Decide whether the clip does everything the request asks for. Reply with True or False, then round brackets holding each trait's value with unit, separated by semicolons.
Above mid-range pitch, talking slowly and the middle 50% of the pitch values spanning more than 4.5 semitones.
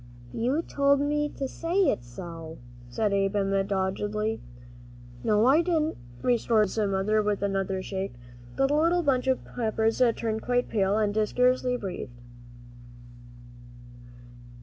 True (220 Hz; 125 wpm; 5.2 semitones)